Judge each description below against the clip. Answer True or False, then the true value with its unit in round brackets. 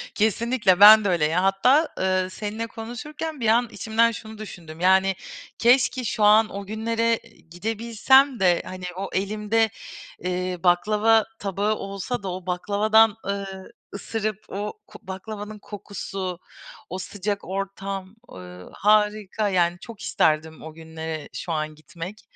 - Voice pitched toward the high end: True (200 Hz)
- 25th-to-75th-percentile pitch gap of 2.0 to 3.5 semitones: True (3.1 semitones)